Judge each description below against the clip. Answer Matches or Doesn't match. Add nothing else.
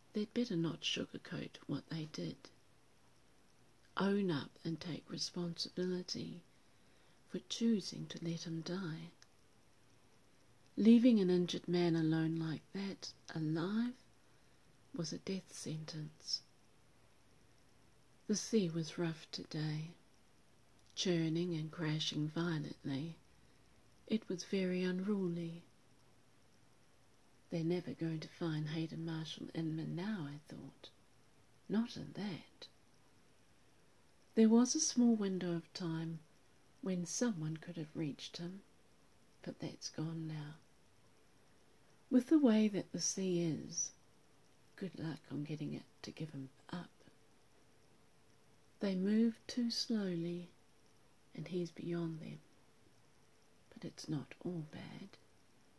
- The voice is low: Doesn't match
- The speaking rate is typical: Doesn't match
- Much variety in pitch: Doesn't match